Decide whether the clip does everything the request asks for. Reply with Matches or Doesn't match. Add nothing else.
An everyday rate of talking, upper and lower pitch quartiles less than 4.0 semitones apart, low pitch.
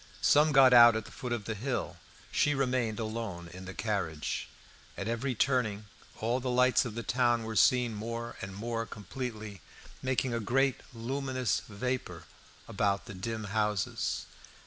Matches